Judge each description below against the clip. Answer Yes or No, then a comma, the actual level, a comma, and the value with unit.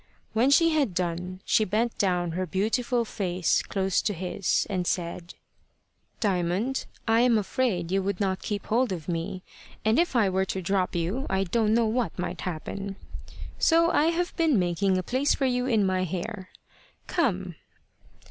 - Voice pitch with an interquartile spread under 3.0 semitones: No, average, 4.6 semitones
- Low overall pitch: No, high, 195 Hz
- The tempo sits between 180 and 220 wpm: No, average, 170 wpm